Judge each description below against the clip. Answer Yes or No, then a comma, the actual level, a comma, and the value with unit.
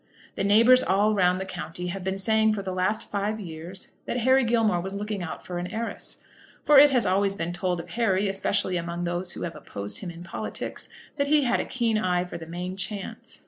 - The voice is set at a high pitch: Yes, high, 195 Hz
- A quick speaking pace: Yes, fast, 225 wpm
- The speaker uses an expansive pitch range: No, average, 3.5 semitones